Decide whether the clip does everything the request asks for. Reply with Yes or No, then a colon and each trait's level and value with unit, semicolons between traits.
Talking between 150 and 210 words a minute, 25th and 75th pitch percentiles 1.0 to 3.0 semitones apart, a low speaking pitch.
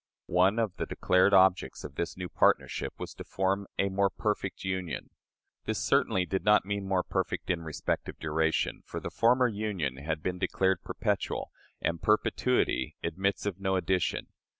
Yes: average, 170 wpm; narrow, 2.5 semitones; very low, 95 Hz